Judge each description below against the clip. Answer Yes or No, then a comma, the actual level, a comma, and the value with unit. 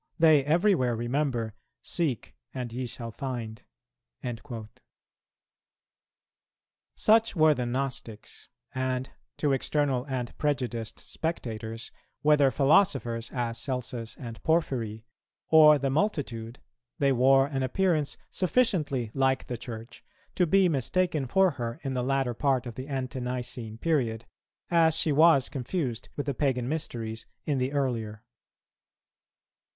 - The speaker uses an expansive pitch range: No, average, 4.0 semitones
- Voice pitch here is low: Yes, low, 130 Hz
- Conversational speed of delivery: No, slow, 120 wpm